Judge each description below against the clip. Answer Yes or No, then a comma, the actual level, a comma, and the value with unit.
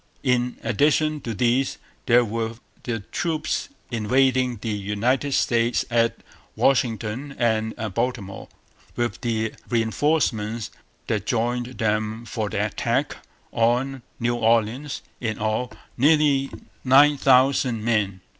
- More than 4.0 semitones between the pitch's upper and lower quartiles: No, average, 3.1 semitones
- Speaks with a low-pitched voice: Yes, low, 120 Hz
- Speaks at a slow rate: Yes, slow, 110 wpm